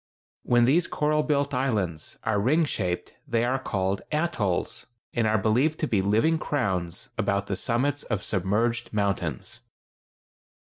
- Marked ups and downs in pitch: Yes, wide, 6.3 semitones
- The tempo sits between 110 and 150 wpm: Yes, average, 140 wpm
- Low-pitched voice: Yes, low, 115 Hz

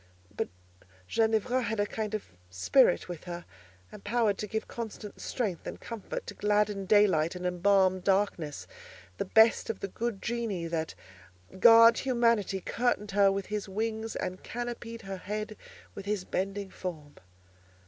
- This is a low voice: No, high, 205 Hz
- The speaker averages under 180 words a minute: Yes, average, 150 wpm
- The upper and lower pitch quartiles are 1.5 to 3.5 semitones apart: Yes, average, 3.0 semitones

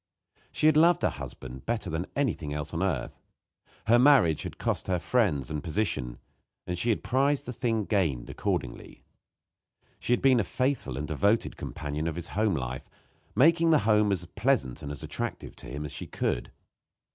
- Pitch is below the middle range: Yes, very low, 95 Hz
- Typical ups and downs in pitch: No, wide, 8.6 semitones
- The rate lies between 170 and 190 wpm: Yes, average, 180 wpm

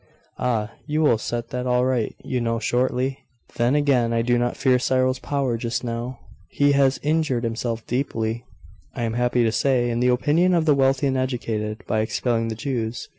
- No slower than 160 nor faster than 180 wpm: No, average, 190 wpm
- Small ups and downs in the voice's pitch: Yes, narrow, 2.3 semitones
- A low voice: Yes, low, 125 Hz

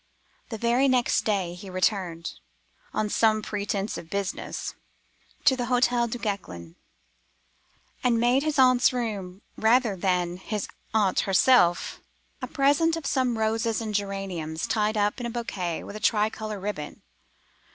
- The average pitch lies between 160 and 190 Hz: No, high, 215 Hz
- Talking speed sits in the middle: No, slow, 130 wpm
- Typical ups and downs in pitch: Yes, average, 4.3 semitones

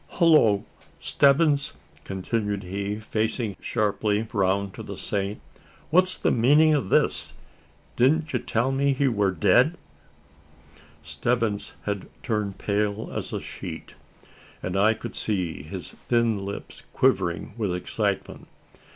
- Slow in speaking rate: Yes, slow, 125 wpm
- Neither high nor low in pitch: No, low, 110 Hz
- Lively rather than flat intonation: No, average, 4.5 semitones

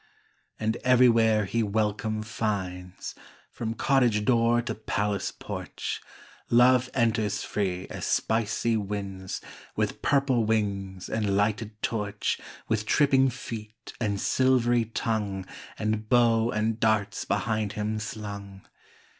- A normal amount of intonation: No, narrow, 2.2 semitones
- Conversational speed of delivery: No, slow, 115 wpm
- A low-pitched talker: Yes, low, 110 Hz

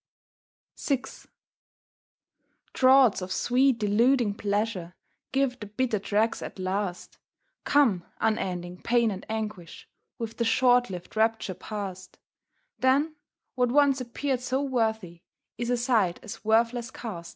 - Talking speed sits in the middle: No, slow, 120 wpm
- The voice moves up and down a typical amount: Yes, average, 3.8 semitones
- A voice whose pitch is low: No, high, 225 Hz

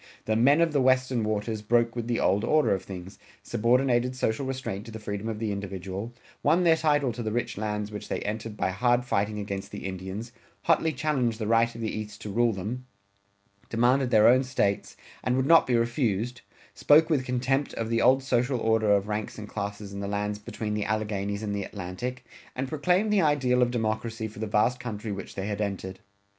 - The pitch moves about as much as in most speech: Yes, average, 3.5 semitones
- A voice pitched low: Yes, low, 115 Hz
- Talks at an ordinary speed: No, fast, 210 wpm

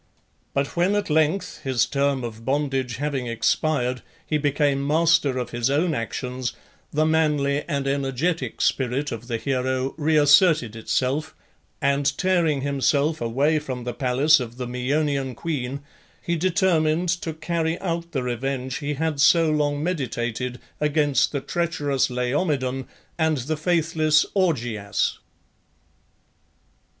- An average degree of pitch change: Yes, average, 3.6 semitones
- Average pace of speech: No, slow, 130 wpm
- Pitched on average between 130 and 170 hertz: Yes, medium, 140 Hz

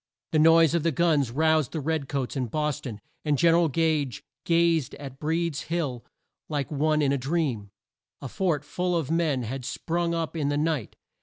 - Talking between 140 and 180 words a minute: No, average, 200 wpm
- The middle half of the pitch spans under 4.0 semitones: Yes, average, 3.2 semitones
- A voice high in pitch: No, medium, 155 Hz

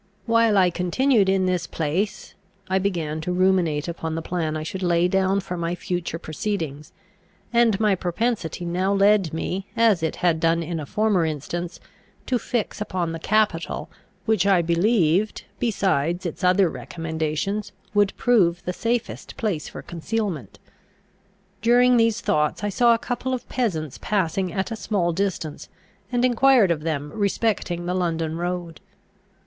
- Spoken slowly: No, average, 155 wpm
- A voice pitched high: No, medium, 180 Hz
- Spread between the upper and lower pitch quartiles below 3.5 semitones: No, average, 4.2 semitones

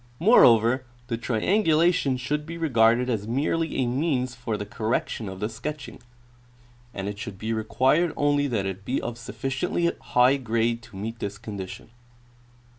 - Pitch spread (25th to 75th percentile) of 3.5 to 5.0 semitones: Yes, average, 4.5 semitones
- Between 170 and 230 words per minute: No, average, 155 wpm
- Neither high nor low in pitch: No, low, 120 Hz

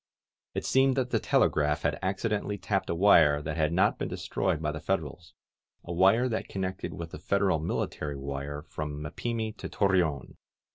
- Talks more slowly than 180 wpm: No, average, 185 wpm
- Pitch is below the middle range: Yes, very low, 85 Hz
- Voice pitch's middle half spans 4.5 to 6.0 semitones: Yes, average, 4.9 semitones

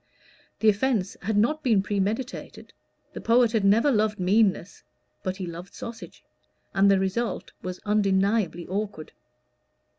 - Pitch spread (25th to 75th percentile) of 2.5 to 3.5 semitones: Yes, average, 2.9 semitones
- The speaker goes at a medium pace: No, slow, 130 wpm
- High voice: Yes, high, 205 Hz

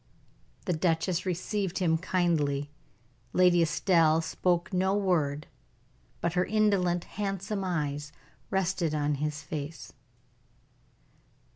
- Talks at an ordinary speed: No, slow, 100 wpm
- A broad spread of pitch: No, average, 3.4 semitones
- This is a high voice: No, medium, 175 Hz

